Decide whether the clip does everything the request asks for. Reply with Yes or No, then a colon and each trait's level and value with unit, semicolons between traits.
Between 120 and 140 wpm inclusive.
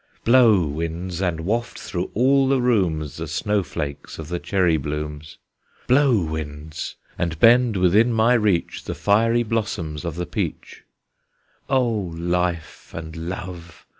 Yes: slow, 135 wpm